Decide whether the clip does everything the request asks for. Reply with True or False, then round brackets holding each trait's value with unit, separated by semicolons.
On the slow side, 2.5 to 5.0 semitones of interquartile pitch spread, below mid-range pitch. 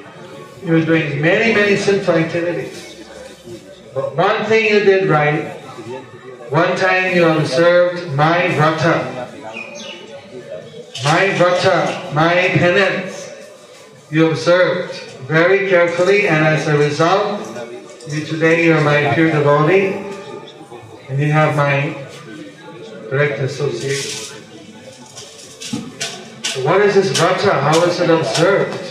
False (110 wpm; 3.7 semitones; 165 Hz)